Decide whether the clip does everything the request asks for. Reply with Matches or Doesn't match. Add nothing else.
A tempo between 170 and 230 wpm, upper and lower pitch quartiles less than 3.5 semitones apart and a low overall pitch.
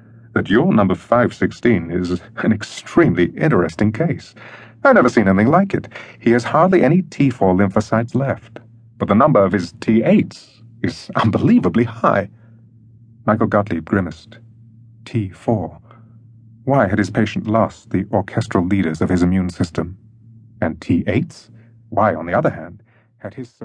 Doesn't match